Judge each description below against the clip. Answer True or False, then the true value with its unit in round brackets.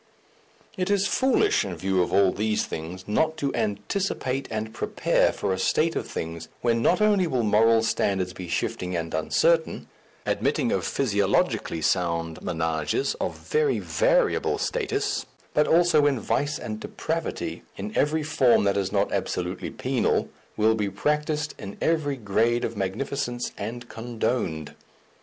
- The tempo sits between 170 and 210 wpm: False (145 wpm)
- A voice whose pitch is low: True (115 Hz)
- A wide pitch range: True (7.7 semitones)